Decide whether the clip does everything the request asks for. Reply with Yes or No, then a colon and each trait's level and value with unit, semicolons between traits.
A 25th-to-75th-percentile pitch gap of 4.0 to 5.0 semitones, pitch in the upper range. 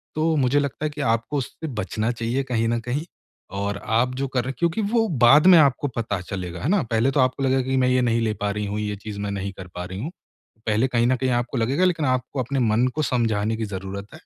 No: average, 4.3 semitones; low, 120 Hz